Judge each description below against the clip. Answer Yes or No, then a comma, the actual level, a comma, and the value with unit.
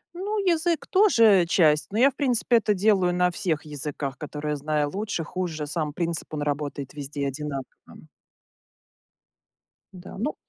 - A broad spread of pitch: Yes, wide, 6.5 semitones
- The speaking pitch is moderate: Yes, medium, 170 Hz